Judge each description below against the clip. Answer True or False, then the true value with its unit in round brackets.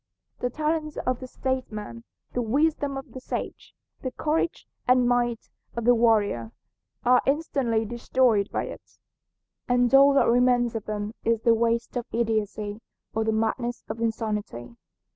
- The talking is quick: False (150 wpm)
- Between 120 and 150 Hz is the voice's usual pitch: False (235 Hz)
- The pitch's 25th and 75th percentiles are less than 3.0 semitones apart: True (2.6 semitones)